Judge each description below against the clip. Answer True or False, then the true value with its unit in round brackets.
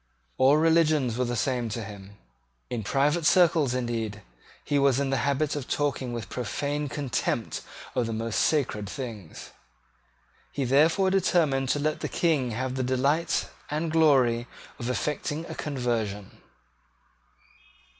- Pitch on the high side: False (135 Hz)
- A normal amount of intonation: True (4.0 semitones)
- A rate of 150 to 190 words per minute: False (140 wpm)